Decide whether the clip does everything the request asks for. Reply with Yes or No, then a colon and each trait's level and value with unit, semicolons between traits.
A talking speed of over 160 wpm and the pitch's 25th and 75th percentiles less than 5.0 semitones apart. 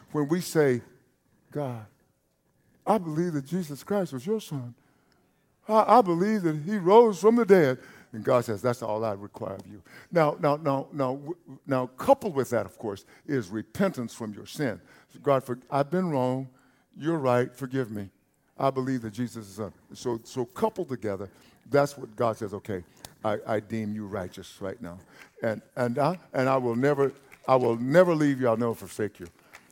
No: average, 185 wpm; average, 5.3 semitones